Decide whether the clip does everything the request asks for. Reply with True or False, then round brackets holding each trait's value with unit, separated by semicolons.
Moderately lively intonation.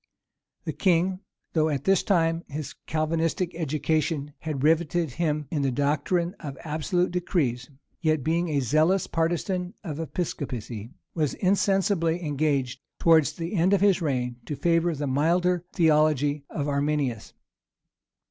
True (3.2 semitones)